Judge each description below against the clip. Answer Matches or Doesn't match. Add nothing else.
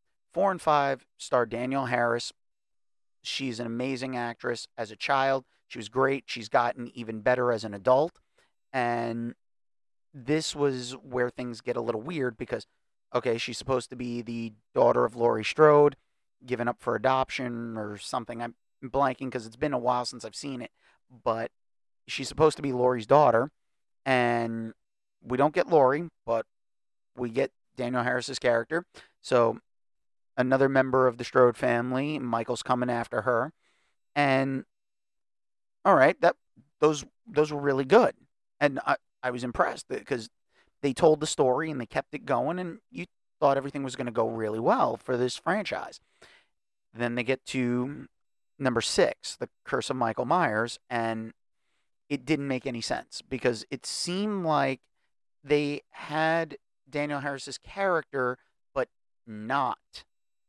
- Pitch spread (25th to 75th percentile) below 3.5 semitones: Matches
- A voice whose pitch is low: Matches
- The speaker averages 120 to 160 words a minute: Matches